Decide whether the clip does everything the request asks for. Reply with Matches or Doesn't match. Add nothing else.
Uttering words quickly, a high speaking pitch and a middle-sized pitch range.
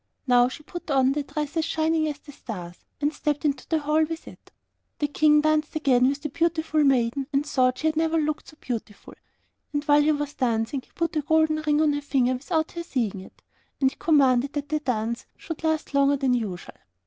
Matches